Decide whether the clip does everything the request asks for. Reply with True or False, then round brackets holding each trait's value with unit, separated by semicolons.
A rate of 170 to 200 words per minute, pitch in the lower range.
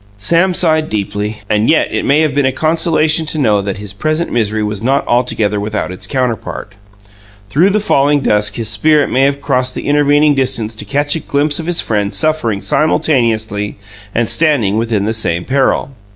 True (185 wpm; 130 Hz)